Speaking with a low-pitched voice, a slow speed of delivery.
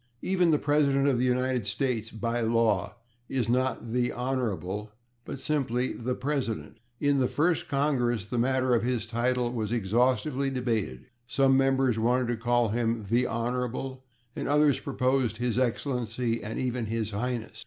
No: low, 125 Hz; average, 155 wpm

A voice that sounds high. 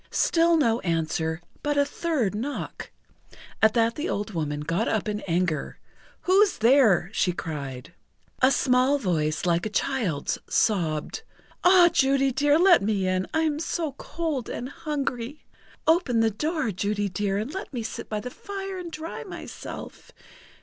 Yes: high, 230 Hz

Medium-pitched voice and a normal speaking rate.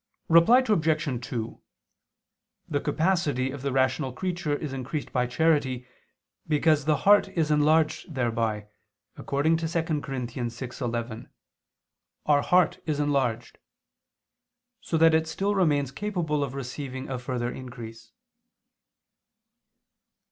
No: medium, 145 Hz; slow, 115 wpm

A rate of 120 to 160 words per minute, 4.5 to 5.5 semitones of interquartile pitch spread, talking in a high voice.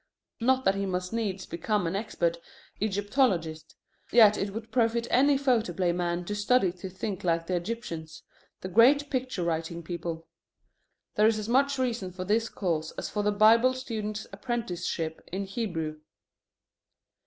Yes: average, 155 wpm; average, 4.8 semitones; high, 205 Hz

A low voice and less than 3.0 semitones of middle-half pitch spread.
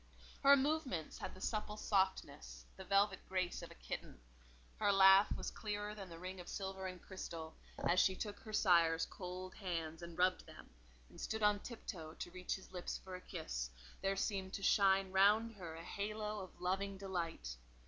No: high, 190 Hz; narrow, 2.6 semitones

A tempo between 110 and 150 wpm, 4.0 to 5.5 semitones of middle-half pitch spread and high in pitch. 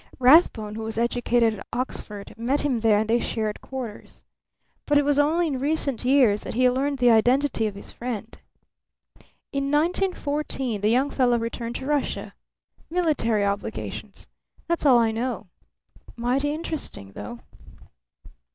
Yes: average, 145 wpm; average, 4.3 semitones; high, 245 Hz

